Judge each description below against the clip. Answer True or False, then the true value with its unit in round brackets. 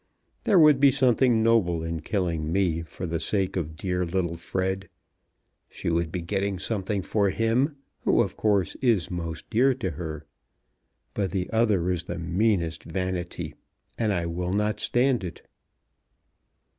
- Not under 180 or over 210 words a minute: False (155 wpm)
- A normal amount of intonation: True (4.5 semitones)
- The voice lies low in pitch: True (95 Hz)